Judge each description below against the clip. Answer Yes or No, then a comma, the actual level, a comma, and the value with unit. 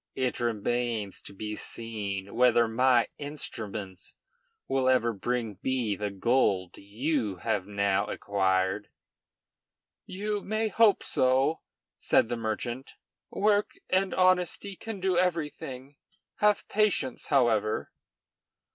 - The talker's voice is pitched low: Yes, low, 120 Hz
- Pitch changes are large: Yes, wide, 7.1 semitones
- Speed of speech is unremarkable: No, slow, 110 wpm